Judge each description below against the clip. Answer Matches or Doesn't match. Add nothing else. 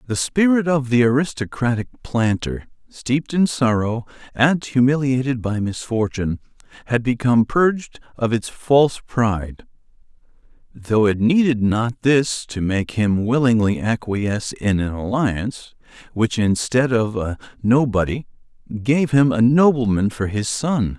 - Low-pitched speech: Matches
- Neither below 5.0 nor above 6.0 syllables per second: Doesn't match